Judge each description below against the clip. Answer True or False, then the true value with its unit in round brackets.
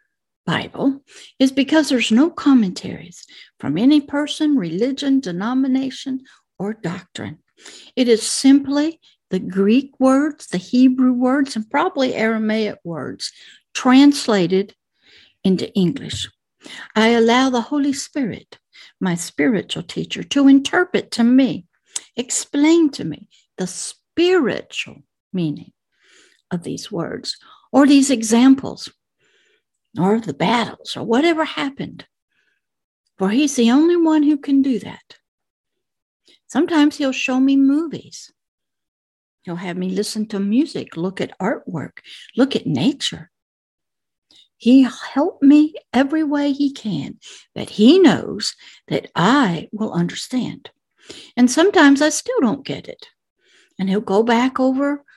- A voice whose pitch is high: True (260 Hz)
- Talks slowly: True (120 wpm)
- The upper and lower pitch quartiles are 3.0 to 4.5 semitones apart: False (5.0 semitones)